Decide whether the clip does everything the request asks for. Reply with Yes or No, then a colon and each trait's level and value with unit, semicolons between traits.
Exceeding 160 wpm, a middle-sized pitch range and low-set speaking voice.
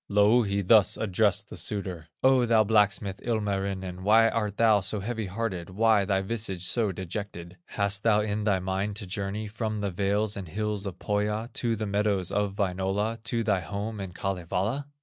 No: average, 175 wpm; narrow, 2.1 semitones; low, 105 Hz